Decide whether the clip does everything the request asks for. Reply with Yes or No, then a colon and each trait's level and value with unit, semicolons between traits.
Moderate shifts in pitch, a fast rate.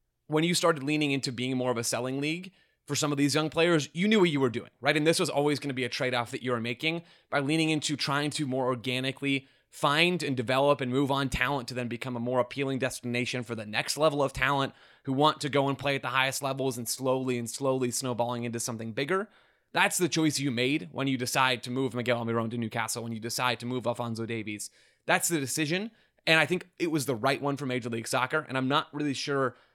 Yes: average, 3.3 semitones; fast, 250 wpm